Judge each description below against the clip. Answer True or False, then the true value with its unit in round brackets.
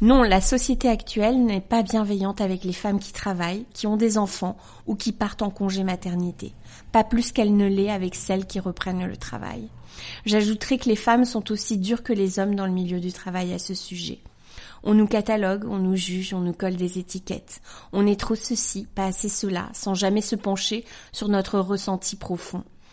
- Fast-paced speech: False (200 wpm)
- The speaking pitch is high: True (200 Hz)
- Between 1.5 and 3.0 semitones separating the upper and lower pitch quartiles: True (2.7 semitones)